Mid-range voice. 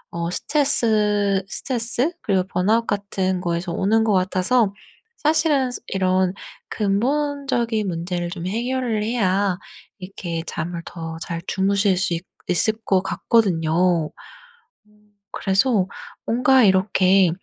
No: high, 195 Hz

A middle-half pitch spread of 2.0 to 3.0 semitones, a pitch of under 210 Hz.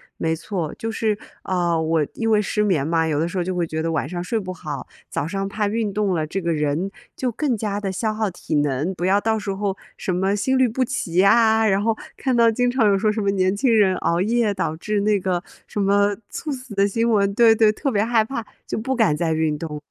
No: average, 4.2 semitones; high, 200 Hz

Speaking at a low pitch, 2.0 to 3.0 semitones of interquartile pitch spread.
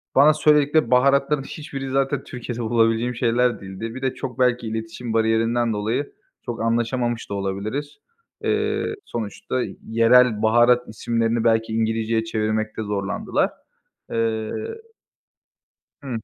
Yes: low, 115 Hz; narrow, 2.4 semitones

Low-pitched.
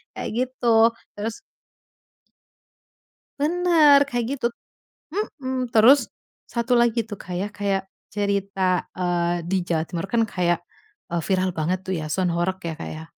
No: high, 200 Hz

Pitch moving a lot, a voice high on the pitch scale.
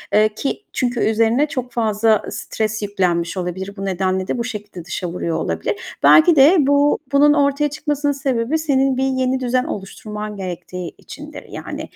Yes: wide, 6.1 semitones; high, 230 Hz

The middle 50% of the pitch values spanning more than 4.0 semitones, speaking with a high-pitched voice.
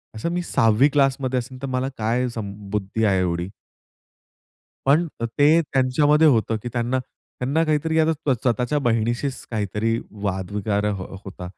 No: average, 5.0 semitones; low, 125 Hz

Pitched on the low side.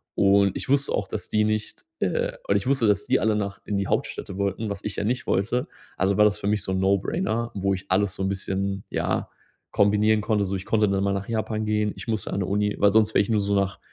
Yes: low, 100 Hz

